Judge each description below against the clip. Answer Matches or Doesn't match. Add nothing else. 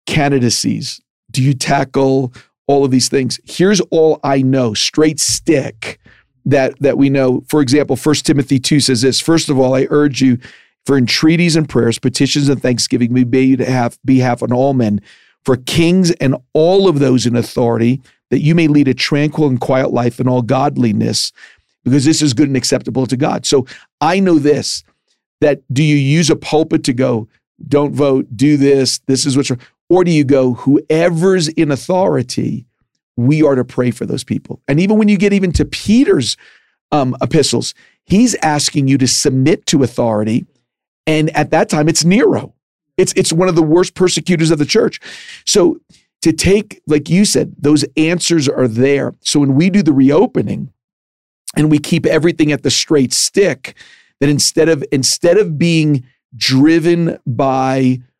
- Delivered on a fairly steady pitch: Doesn't match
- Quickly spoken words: Doesn't match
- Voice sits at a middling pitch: Matches